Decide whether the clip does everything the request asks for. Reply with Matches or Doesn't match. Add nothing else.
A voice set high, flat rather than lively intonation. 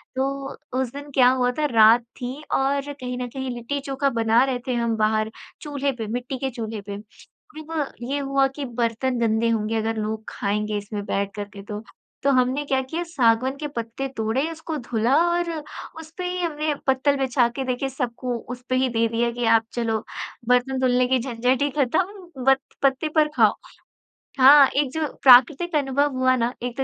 Doesn't match